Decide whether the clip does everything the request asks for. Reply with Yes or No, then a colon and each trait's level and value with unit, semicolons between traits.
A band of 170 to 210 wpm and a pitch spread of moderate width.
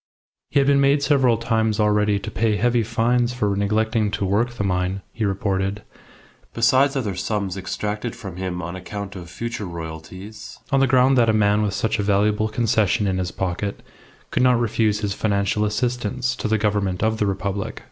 Yes: average, 190 wpm; average, 3.0 semitones